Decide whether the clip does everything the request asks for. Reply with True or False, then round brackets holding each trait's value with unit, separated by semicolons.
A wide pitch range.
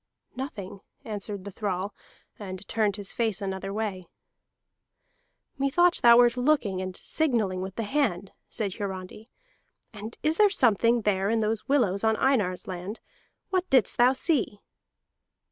False (4.2 semitones)